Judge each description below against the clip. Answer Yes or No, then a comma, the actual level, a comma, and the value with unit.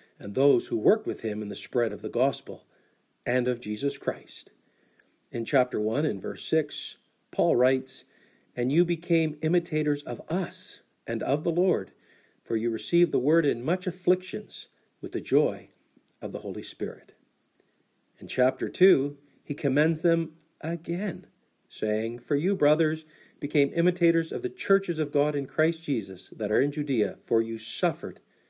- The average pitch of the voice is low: No, medium, 150 Hz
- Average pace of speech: Yes, average, 160 wpm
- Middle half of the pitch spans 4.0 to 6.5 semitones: Yes, average, 4.9 semitones